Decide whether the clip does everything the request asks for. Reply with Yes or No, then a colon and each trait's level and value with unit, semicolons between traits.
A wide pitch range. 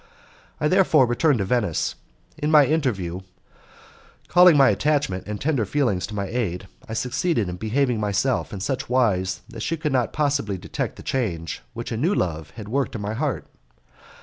Yes: wide, 5.9 semitones